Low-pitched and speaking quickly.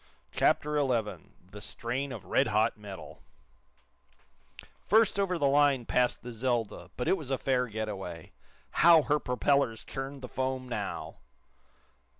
No: low, 125 Hz; average, 145 wpm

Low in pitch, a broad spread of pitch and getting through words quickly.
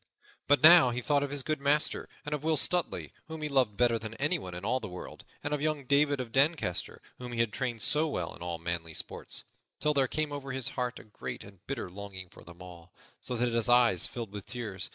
Yes: low, 125 Hz; wide, 6.3 semitones; fast, 235 wpm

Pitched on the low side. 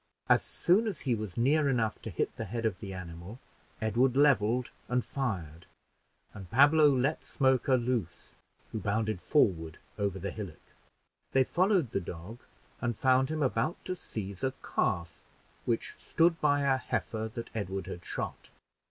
Yes: low, 115 Hz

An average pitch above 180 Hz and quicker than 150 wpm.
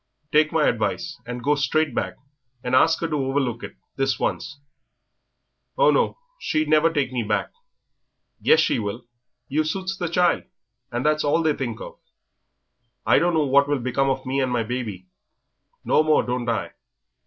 No: medium, 140 Hz; average, 175 wpm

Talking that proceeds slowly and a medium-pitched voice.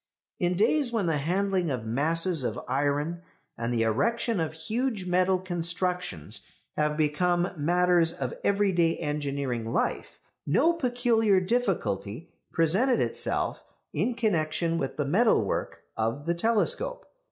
Yes: slow, 130 wpm; medium, 175 Hz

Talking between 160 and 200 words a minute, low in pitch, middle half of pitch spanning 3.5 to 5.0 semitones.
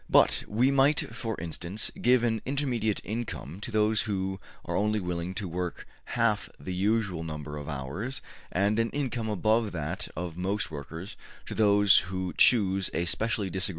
Yes: average, 170 wpm; low, 100 Hz; average, 4.0 semitones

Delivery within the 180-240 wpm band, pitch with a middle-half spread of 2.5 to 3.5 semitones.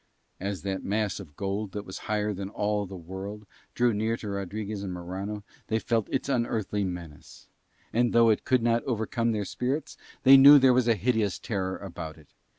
Yes: average, 190 wpm; average, 3.1 semitones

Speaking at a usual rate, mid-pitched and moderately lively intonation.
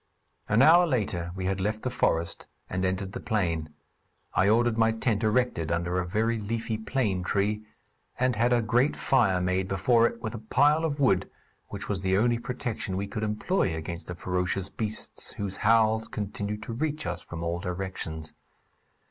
No: average, 180 wpm; low, 105 Hz; average, 3.9 semitones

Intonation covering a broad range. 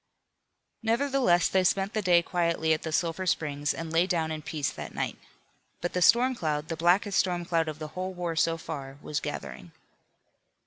No: average, 2.7 semitones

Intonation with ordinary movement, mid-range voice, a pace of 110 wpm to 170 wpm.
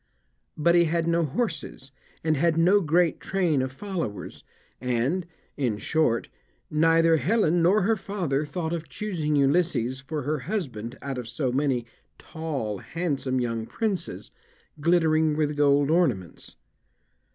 Yes: average, 4.4 semitones; medium, 155 Hz; slow, 135 wpm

